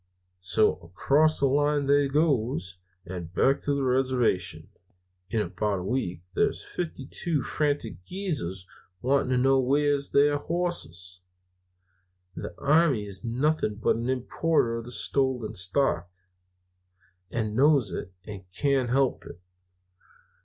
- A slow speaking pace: Yes, slow, 125 wpm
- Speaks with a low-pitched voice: Yes, low, 130 Hz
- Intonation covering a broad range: Yes, wide, 6.2 semitones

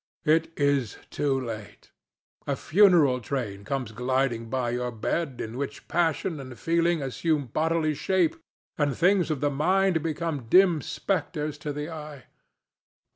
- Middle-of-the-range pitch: Yes, medium, 145 Hz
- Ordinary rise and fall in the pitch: Yes, average, 4.3 semitones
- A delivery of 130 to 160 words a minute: Yes, average, 140 wpm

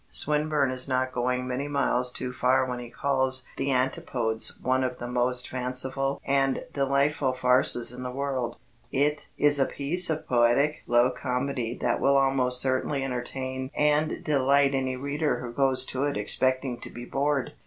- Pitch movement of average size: No, narrow, 1.8 semitones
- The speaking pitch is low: Yes, low, 130 Hz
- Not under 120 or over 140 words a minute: No, average, 165 wpm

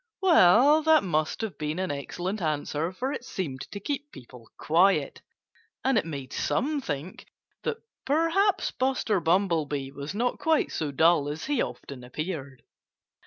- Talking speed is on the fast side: No, average, 150 wpm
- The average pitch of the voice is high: No, medium, 180 Hz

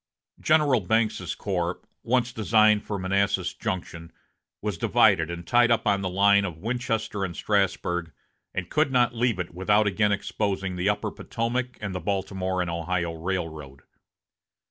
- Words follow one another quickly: No, average, 150 wpm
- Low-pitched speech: Yes, low, 100 Hz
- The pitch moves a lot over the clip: No, average, 3.8 semitones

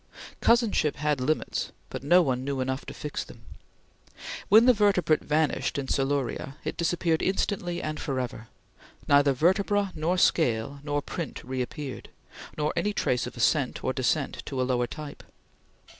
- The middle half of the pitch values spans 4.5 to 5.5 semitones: Yes, average, 4.9 semitones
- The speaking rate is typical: Yes, average, 150 wpm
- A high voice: No, medium, 150 Hz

